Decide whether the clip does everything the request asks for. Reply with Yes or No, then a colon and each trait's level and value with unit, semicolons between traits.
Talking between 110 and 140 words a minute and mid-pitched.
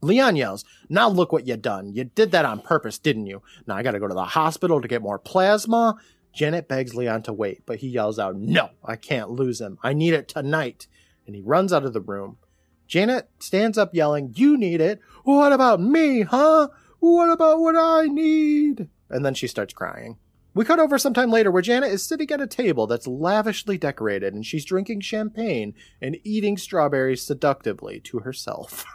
No: average, 200 wpm; medium, 170 Hz